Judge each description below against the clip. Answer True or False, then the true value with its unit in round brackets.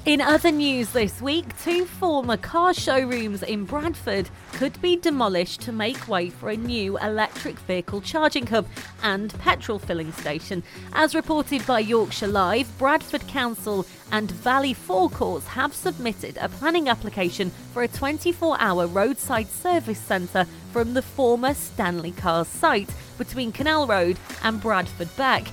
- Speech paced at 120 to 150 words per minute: True (145 wpm)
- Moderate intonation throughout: False (7.0 semitones)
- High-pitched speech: True (230 Hz)